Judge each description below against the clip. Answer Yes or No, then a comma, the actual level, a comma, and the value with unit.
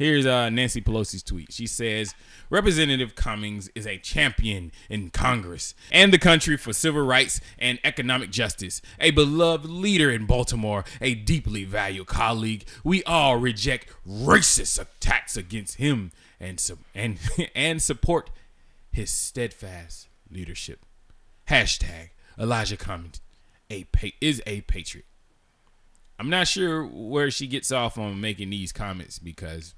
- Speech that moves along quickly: No, slow, 135 wpm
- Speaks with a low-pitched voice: Yes, low, 110 Hz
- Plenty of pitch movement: Yes, wide, 6.2 semitones